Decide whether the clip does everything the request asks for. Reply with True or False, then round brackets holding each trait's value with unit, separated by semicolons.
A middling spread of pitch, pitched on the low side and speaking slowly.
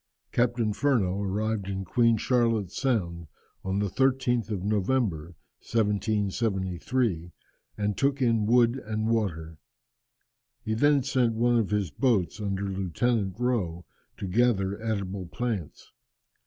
True (3.9 semitones; 105 Hz; 120 wpm)